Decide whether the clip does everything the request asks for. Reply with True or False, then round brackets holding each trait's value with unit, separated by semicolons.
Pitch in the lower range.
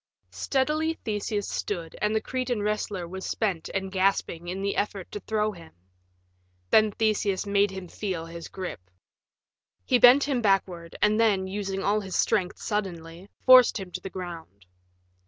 False (200 Hz)